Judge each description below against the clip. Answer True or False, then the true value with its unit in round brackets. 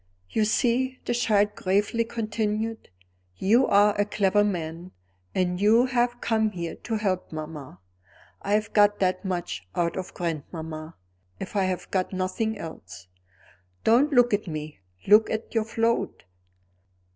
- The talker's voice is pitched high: True (205 Hz)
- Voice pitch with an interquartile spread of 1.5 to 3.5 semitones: False (3.9 semitones)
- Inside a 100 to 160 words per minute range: True (145 wpm)